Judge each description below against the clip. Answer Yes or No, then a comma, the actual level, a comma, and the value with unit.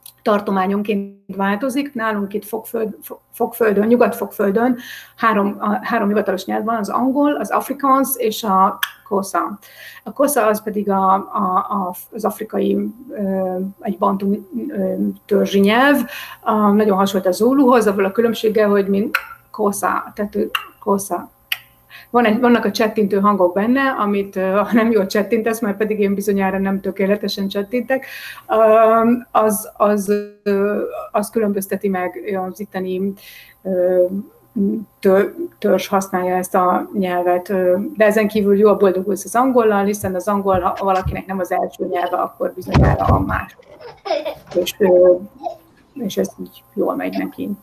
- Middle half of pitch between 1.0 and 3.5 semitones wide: Yes, average, 2.7 semitones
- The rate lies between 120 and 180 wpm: Yes, average, 130 wpm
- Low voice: No, high, 205 Hz